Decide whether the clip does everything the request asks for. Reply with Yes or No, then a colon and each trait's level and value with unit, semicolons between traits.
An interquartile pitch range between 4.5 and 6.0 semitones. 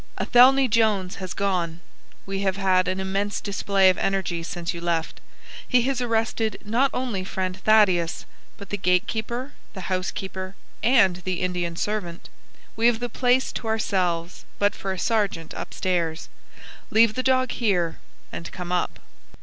No: average, 3.7 semitones